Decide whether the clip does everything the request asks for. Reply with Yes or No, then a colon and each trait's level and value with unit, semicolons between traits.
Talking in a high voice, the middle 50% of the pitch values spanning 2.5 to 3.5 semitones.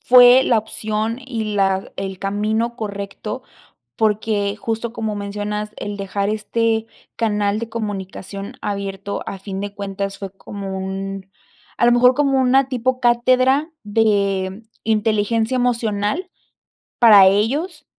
Yes: high, 210 Hz; average, 2.9 semitones